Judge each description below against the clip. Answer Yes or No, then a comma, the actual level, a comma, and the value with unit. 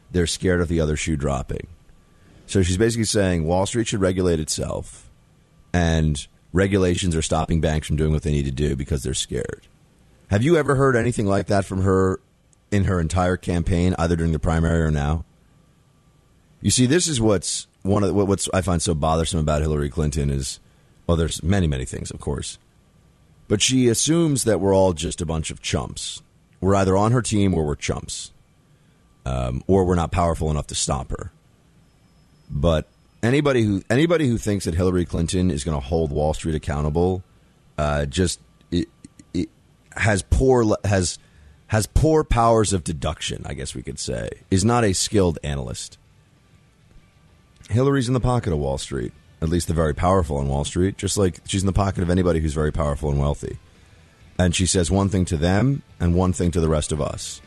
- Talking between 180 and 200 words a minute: Yes, average, 195 wpm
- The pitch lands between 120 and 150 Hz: No, very low, 90 Hz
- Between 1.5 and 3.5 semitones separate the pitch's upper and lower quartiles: No, average, 4.1 semitones